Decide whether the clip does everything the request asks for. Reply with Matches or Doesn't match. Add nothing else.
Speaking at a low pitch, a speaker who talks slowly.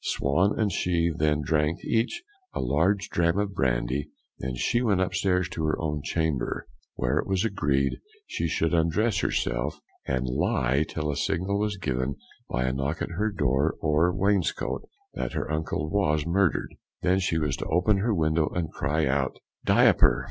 Doesn't match